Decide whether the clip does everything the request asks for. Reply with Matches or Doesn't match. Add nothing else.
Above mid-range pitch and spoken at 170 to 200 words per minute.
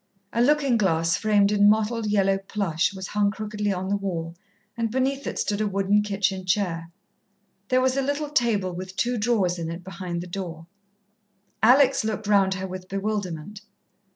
Matches